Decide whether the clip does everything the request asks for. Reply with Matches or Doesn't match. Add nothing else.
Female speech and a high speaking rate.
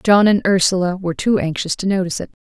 Matches